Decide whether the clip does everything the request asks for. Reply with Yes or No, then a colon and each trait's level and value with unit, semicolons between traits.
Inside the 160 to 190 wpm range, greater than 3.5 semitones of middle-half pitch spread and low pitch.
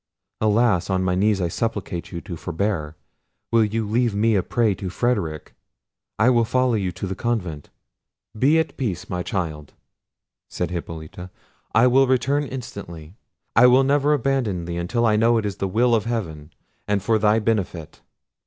Yes: average, 170 wpm; average, 4.9 semitones; low, 105 Hz